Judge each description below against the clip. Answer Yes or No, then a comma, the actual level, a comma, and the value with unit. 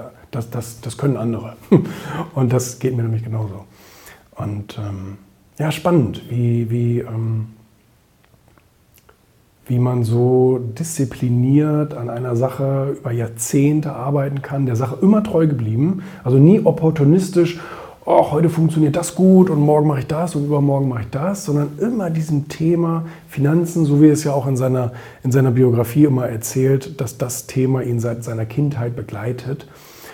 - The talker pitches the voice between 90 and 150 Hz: Yes, low, 135 Hz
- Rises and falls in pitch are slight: No, average, 4.3 semitones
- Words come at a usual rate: Yes, average, 155 wpm